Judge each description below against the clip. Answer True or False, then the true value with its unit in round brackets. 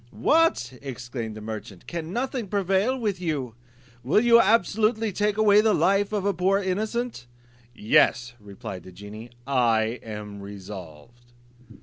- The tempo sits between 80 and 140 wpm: True (135 wpm)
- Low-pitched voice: False (145 Hz)